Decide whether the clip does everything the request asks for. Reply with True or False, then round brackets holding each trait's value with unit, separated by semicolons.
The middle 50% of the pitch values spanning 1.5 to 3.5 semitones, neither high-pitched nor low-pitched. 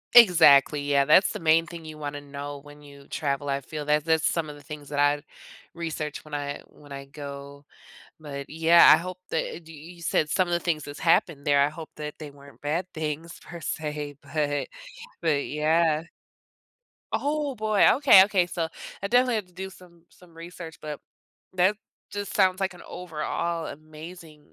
True (3.0 semitones; 155 Hz)